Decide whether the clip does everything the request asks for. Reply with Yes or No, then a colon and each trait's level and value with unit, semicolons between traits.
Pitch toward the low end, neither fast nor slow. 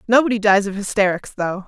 No: high, 205 Hz; average, 180 wpm